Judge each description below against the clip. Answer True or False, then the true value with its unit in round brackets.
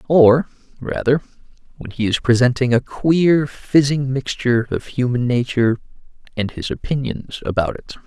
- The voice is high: False (130 Hz)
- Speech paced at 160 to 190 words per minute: False (135 wpm)